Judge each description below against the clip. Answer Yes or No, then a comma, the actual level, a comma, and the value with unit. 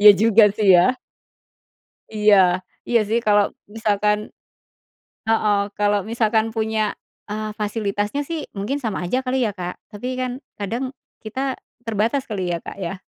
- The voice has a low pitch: No, high, 215 Hz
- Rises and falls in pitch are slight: Yes, narrow, 2.3 semitones